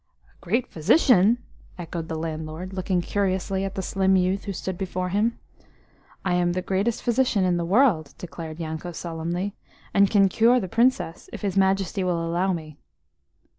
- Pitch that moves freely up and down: No, average, 2.7 semitones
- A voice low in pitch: No, medium, 185 Hz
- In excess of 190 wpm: No, average, 170 wpm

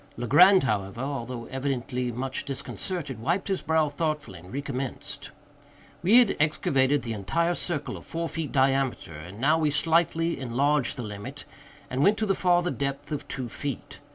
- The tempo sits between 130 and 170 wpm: Yes, average, 160 wpm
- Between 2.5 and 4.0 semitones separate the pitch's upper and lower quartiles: No, average, 4.6 semitones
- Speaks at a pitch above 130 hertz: Yes, medium, 140 Hz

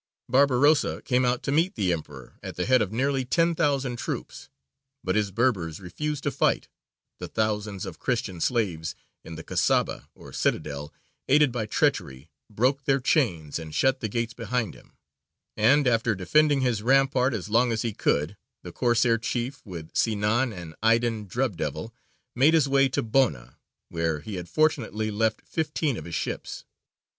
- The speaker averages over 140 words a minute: Yes, average, 170 wpm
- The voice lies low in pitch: Yes, low, 115 Hz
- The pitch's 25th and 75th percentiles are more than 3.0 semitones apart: Yes, average, 5.3 semitones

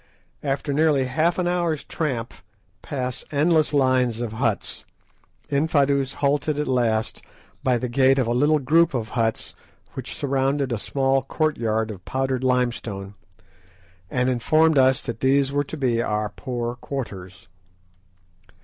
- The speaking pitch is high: No, low, 130 Hz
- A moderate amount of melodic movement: Yes, average, 3.2 semitones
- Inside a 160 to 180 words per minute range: No, average, 140 wpm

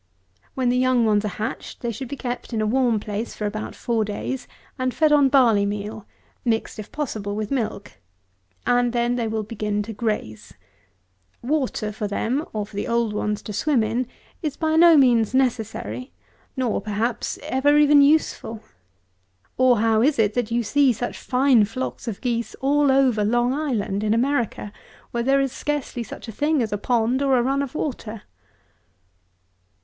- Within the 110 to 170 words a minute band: No, average, 180 wpm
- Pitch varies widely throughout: No, average, 3.6 semitones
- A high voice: Yes, high, 240 Hz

